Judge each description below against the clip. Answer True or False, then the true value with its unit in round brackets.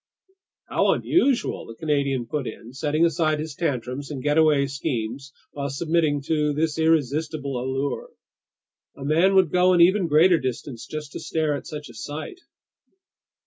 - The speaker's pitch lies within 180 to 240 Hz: False (150 Hz)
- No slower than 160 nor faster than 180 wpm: False (150 wpm)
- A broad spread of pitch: False (2.7 semitones)